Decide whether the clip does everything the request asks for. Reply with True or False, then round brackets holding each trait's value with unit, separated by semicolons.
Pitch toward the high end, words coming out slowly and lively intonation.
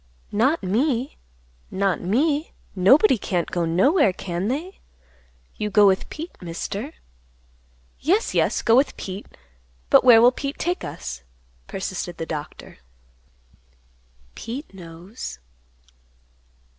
True (210 Hz; 110 wpm; 7.4 semitones)